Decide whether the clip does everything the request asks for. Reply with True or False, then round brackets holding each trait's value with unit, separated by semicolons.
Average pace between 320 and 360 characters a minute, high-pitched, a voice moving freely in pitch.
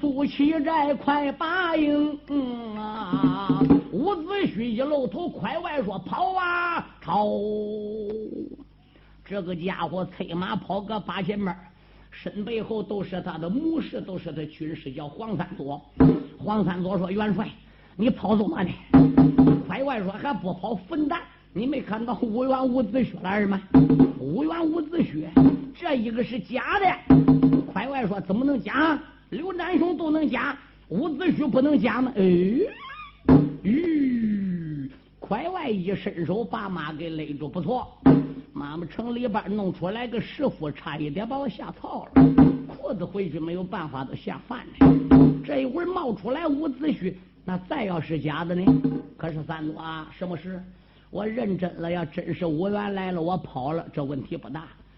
False (220 characters per minute; 205 Hz; 8.0 semitones)